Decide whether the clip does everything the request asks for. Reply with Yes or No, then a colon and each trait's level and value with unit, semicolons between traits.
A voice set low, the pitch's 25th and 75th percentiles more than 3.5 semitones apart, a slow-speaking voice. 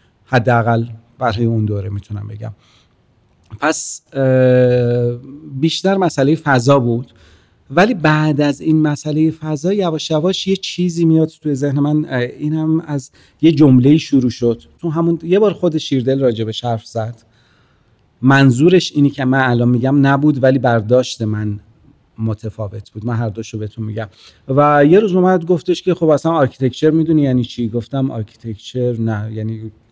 No: low, 130 Hz; wide, 5.4 semitones; average, 150 wpm